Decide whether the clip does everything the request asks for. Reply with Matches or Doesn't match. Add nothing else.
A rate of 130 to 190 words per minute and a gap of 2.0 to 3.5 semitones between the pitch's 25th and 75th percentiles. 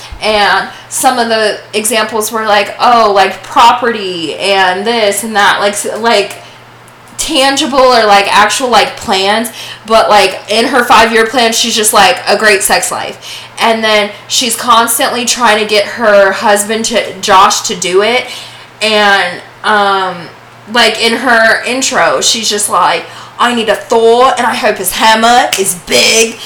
Matches